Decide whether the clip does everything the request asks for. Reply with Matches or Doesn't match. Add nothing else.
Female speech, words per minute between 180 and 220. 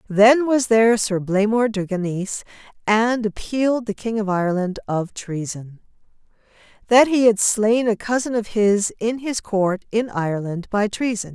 Doesn't match